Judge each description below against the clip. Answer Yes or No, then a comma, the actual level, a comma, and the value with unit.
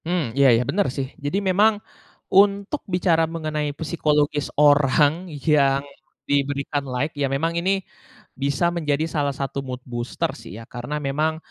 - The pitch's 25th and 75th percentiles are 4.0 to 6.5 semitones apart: No, average, 3.3 semitones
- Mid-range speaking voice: Yes, medium, 150 Hz